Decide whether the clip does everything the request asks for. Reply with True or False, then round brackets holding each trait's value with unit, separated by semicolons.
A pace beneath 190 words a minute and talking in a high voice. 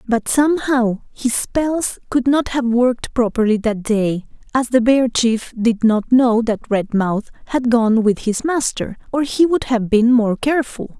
True (175 wpm; 240 Hz)